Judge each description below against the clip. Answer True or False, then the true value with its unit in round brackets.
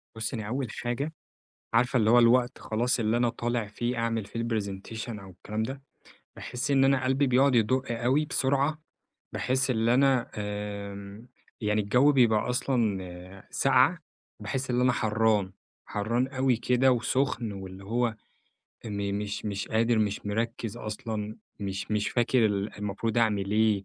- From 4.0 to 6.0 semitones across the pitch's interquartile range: False (3.4 semitones)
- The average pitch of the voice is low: True (115 Hz)